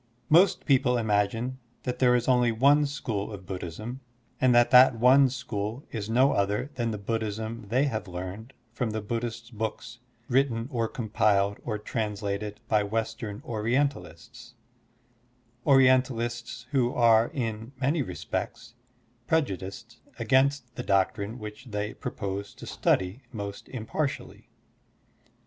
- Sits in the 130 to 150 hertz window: No, low, 115 Hz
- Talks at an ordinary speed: No, slow, 130 wpm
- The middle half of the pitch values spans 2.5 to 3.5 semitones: Yes, average, 3.1 semitones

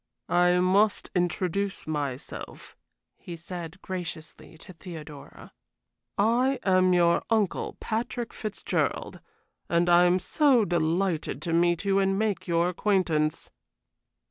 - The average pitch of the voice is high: No, medium, 180 Hz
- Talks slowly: Yes, slow, 115 wpm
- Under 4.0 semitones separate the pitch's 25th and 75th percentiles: Yes, average, 2.8 semitones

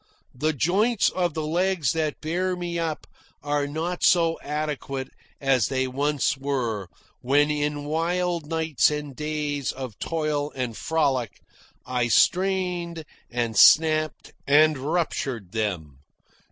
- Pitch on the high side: No, medium, 150 Hz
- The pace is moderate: No, slow, 125 wpm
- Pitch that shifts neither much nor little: Yes, average, 3.6 semitones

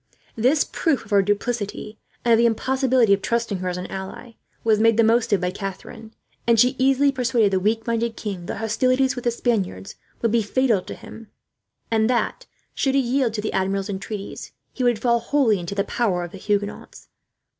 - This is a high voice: Yes, high, 225 Hz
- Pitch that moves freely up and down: No, average, 3.4 semitones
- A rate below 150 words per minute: No, average, 200 wpm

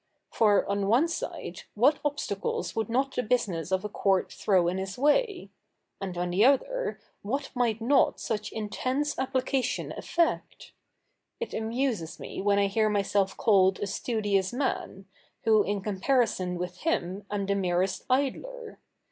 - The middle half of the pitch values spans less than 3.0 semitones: No, average, 5.3 semitones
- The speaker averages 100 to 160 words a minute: Yes, average, 150 wpm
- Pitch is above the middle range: Yes, high, 215 Hz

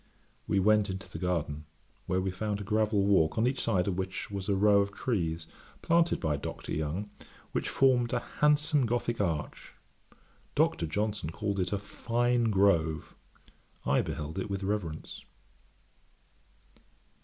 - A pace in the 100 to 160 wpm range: Yes, average, 150 wpm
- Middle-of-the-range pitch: No, low, 100 Hz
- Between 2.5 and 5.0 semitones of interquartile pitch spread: Yes, average, 3.4 semitones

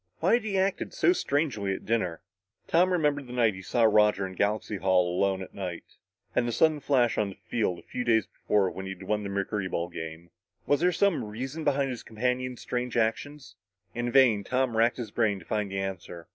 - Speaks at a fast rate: Yes, fast, 215 wpm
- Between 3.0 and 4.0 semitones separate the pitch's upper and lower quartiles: No, wide, 5.5 semitones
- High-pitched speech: No, low, 110 Hz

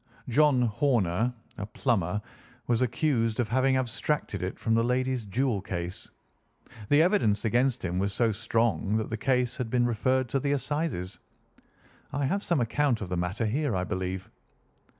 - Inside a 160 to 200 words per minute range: Yes, average, 165 wpm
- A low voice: Yes, low, 120 Hz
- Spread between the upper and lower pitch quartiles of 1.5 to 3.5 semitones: No, average, 4.3 semitones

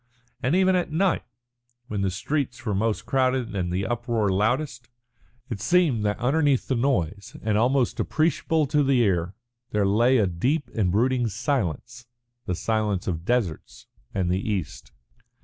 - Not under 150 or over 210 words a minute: Yes, average, 155 wpm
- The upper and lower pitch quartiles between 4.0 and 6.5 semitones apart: Yes, average, 5.1 semitones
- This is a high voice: No, low, 115 Hz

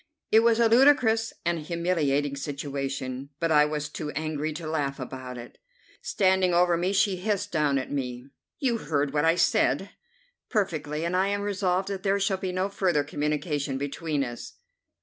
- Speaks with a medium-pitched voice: Yes, medium, 160 Hz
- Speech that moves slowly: No, average, 170 wpm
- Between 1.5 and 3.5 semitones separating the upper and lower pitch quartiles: No, average, 5.1 semitones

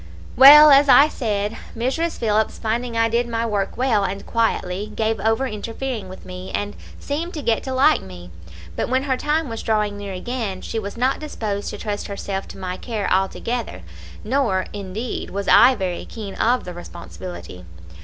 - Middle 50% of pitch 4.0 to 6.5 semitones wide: Yes, average, 4.3 semitones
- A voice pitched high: Yes, high, 220 Hz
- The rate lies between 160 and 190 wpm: Yes, average, 180 wpm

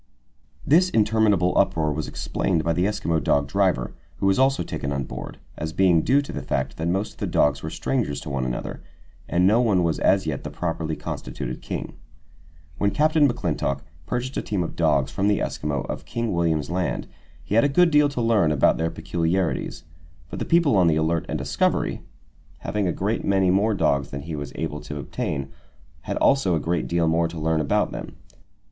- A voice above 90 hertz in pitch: No, very low, 85 Hz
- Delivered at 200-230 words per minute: Yes, fast, 205 wpm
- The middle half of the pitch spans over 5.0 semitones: Yes, wide, 5.4 semitones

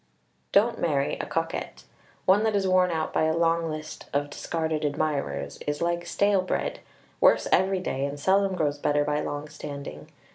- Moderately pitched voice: Yes, medium, 160 Hz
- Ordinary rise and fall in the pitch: Yes, average, 4.2 semitones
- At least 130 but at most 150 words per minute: No, average, 175 wpm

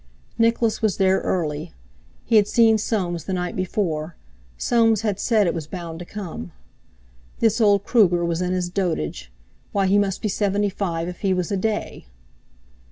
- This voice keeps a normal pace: Yes, average, 165 wpm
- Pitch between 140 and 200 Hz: Yes, high, 190 Hz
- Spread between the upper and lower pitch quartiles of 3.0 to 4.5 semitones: Yes, average, 3.6 semitones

